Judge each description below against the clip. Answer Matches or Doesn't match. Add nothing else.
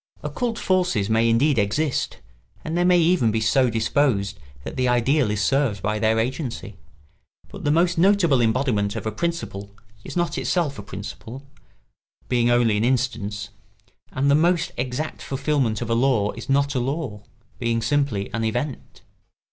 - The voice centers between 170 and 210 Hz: Doesn't match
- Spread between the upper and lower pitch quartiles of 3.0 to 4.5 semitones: Doesn't match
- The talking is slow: Doesn't match